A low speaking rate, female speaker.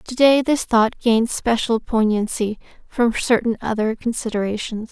Yes: slow, 120 wpm; female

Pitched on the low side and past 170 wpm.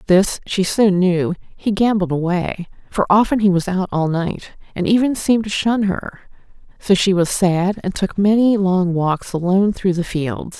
No: high, 190 Hz; average, 185 wpm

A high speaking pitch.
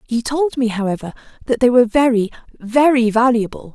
Yes: high, 240 Hz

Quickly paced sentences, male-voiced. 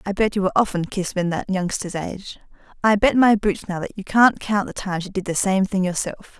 No: fast, 255 wpm; female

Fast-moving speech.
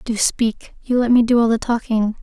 Yes: fast, 240 wpm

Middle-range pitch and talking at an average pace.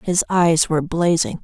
Yes: medium, 165 Hz; average, 165 wpm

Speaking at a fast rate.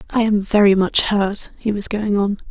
Yes: fast, 215 wpm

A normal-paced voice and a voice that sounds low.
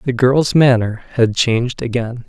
Yes: average, 160 wpm; low, 120 Hz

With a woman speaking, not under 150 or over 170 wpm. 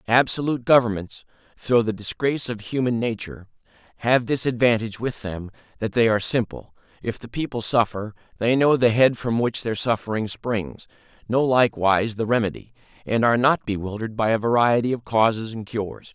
No: male; average, 165 wpm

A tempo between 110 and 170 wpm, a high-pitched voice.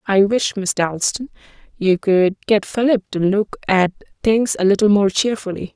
Yes: average, 165 wpm; high, 200 Hz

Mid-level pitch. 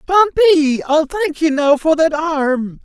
No: very high, 310 Hz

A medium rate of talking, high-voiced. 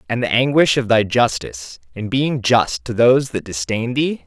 No: average, 195 wpm; low, 120 Hz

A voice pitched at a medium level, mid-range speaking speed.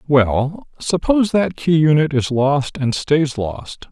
Yes: medium, 150 Hz; average, 155 wpm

